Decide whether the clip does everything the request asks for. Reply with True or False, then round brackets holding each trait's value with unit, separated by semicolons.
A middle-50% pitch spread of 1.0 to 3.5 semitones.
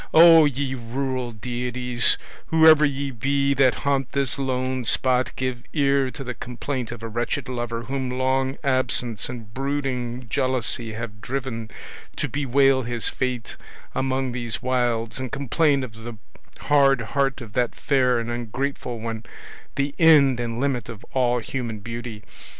True (2.5 semitones)